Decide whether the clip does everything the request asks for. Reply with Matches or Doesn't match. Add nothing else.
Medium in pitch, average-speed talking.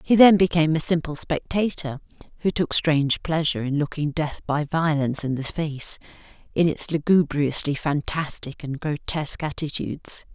Matches